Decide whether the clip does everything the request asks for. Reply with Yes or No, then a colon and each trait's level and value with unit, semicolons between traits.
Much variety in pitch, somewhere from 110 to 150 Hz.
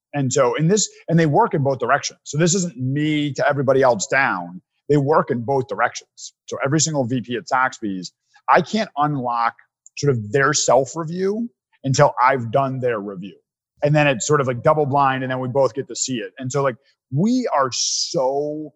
No: average, 3.4 semitones; medium, 140 Hz